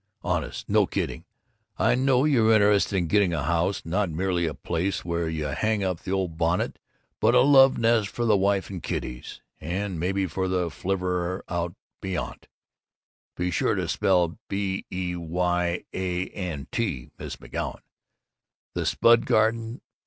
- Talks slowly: No, average, 160 wpm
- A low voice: Yes, very low, 95 Hz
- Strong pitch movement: No, average, 3.1 semitones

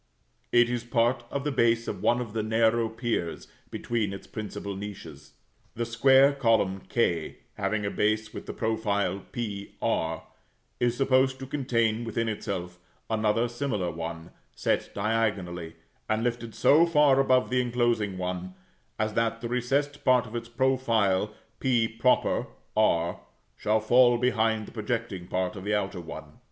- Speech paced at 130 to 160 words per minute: Yes, average, 150 wpm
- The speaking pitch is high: No, low, 115 Hz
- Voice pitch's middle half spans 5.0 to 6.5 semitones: No, average, 3.2 semitones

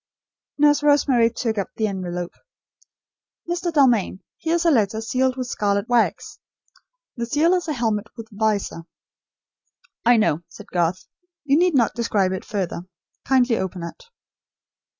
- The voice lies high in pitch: Yes, high, 230 Hz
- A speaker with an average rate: Yes, average, 150 wpm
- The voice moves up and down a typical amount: No, wide, 6.1 semitones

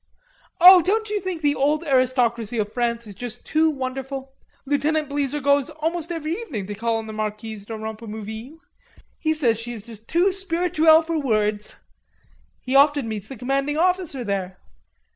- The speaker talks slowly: No, average, 165 wpm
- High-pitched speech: Yes, very high, 270 Hz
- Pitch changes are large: Yes, wide, 5.9 semitones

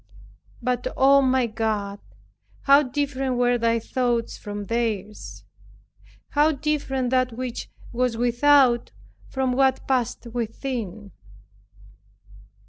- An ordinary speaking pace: No, slow, 100 wpm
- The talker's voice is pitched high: Yes, high, 245 Hz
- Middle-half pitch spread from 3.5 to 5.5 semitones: No, narrow, 2.6 semitones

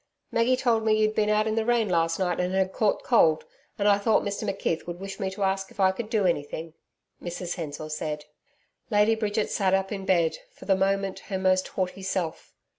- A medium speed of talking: No, fast, 215 wpm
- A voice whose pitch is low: No, high, 195 Hz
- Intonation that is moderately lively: Yes, average, 3.0 semitones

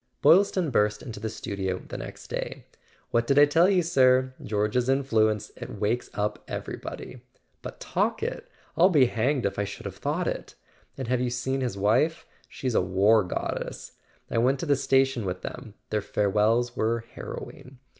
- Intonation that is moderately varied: Yes, average, 4.2 semitones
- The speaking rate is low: No, average, 165 wpm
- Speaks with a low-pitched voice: Yes, low, 120 Hz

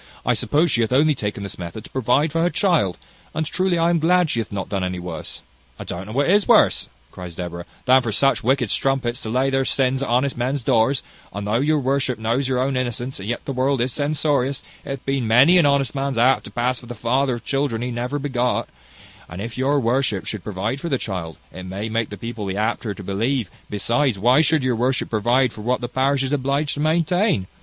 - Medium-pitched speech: No, low, 125 Hz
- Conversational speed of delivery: No, fast, 235 wpm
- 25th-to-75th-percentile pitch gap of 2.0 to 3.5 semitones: No, average, 4.0 semitones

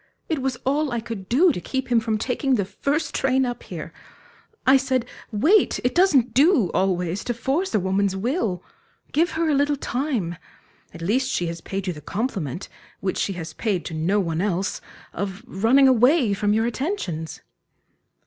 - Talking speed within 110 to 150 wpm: No, average, 180 wpm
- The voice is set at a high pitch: Yes, high, 230 Hz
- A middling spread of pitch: No, wide, 6.0 semitones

